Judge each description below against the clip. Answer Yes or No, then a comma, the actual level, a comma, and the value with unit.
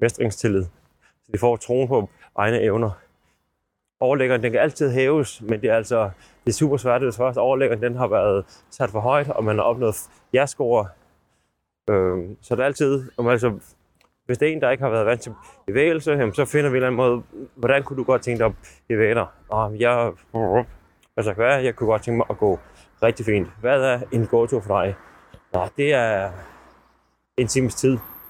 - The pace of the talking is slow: No, average, 195 wpm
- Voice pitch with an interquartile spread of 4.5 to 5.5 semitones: No, average, 3.7 semitones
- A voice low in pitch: Yes, low, 120 Hz